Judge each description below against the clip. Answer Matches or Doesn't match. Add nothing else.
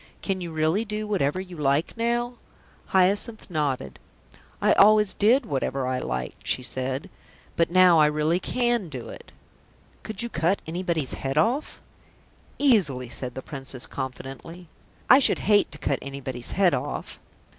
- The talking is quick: Doesn't match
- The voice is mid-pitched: Matches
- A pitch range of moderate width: Doesn't match